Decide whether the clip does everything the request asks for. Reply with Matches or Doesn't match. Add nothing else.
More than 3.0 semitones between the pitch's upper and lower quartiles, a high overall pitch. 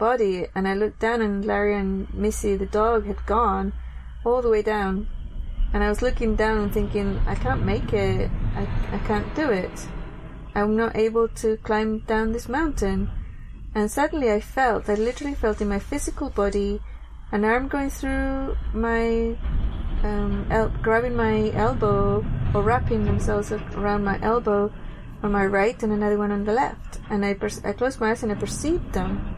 Doesn't match